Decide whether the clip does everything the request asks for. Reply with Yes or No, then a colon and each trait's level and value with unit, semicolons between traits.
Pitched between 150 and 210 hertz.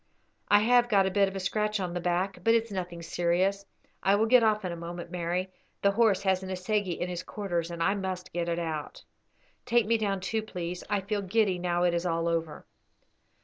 Yes: high, 190 Hz